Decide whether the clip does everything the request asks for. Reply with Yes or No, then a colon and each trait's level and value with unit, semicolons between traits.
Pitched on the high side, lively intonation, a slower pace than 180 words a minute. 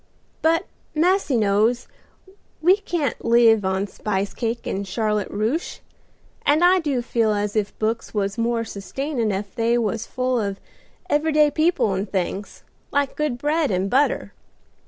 Yes: high, 230 Hz; wide, 6.2 semitones; average, 150 wpm